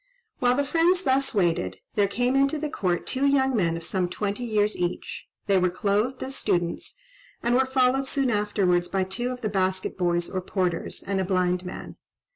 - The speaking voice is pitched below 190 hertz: No, high, 205 Hz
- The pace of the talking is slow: No, average, 195 wpm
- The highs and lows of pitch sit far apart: Yes, wide, 6.2 semitones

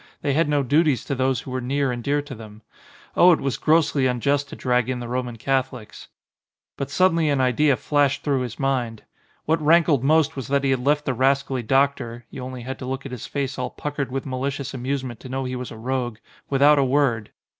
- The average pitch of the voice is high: No, low, 135 Hz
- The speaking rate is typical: No, fast, 225 wpm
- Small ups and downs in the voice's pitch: Yes, narrow, 2.2 semitones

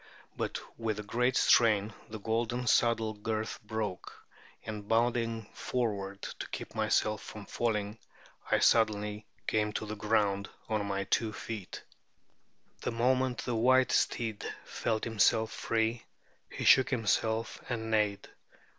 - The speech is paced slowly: Yes, slow, 130 wpm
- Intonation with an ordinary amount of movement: No, narrow, 1.7 semitones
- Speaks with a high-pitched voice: No, low, 110 Hz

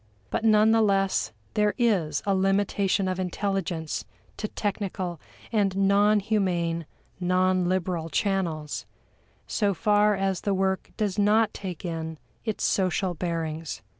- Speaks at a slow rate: Yes, slow, 130 wpm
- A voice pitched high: Yes, high, 195 Hz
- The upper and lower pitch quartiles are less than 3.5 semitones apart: Yes, average, 2.8 semitones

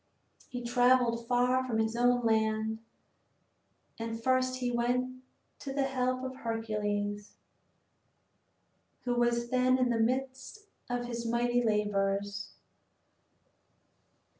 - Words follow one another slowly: Yes, slow, 110 wpm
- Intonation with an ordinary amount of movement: No, narrow, 2.3 semitones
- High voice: Yes, high, 240 Hz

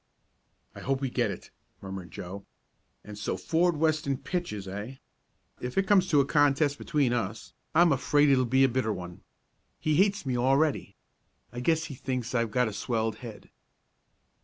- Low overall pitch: Yes, low, 130 Hz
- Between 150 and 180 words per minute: Yes, average, 175 wpm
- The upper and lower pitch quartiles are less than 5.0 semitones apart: No, wide, 5.5 semitones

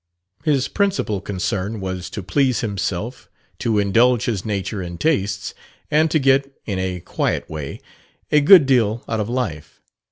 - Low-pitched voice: Yes, low, 110 Hz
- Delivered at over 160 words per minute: No, average, 155 wpm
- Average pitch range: No, wide, 5.9 semitones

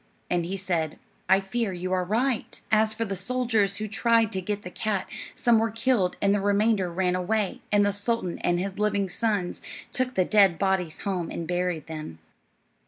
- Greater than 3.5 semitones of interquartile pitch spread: No, average, 3.2 semitones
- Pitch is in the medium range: No, high, 195 Hz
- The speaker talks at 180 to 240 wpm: Yes, average, 190 wpm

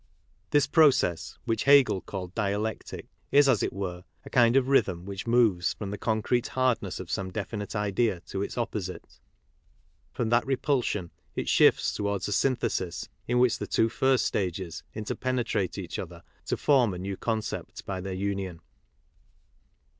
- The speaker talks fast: No, average, 155 wpm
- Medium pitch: No, low, 105 Hz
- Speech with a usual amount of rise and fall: Yes, average, 4.4 semitones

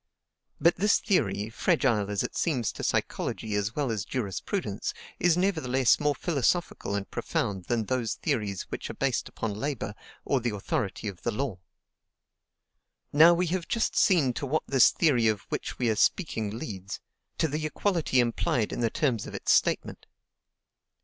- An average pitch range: No, wide, 7.0 semitones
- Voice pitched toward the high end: No, low, 125 Hz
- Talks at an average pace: Yes, average, 165 wpm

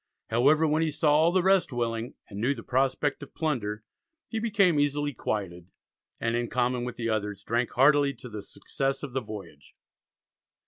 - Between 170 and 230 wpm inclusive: Yes, average, 180 wpm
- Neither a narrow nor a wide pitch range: Yes, average, 4.5 semitones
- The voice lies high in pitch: No, low, 130 Hz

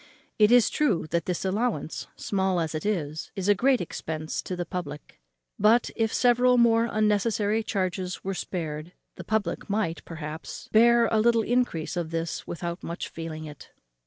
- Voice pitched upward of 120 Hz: Yes, high, 190 Hz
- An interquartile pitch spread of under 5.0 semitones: No, average, 5.3 semitones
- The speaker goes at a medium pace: Yes, average, 165 wpm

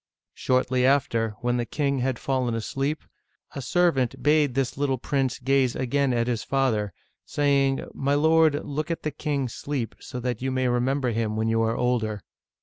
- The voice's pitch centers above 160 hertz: No, low, 130 Hz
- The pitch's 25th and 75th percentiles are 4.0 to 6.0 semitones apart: No, average, 2.7 semitones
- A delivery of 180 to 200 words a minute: Yes, average, 185 wpm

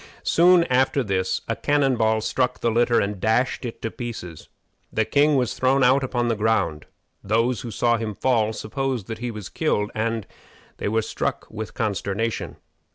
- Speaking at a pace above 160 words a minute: Yes, average, 175 wpm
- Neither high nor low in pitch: No, low, 115 Hz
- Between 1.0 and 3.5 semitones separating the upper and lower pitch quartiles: Yes, average, 3.0 semitones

